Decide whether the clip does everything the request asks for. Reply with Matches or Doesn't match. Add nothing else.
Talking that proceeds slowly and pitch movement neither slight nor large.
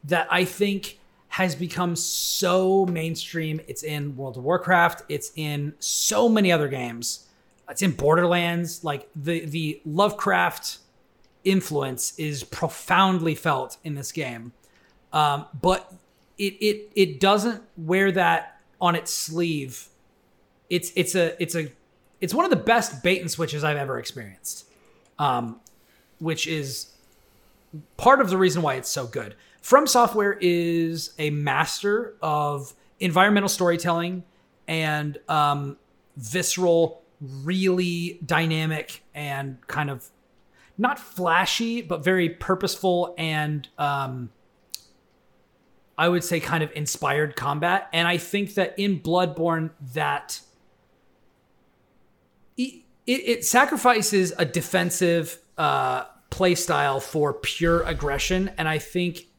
Matches